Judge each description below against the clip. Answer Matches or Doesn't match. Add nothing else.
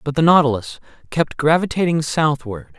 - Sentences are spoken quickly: Doesn't match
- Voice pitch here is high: Doesn't match